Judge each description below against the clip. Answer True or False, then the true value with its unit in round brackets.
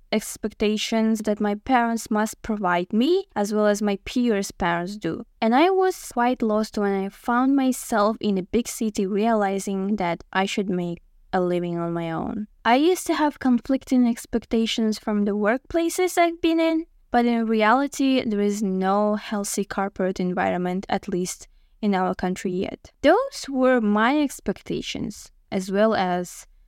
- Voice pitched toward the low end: False (215 Hz)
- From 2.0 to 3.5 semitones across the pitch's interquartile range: False (3.9 semitones)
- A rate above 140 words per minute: True (160 wpm)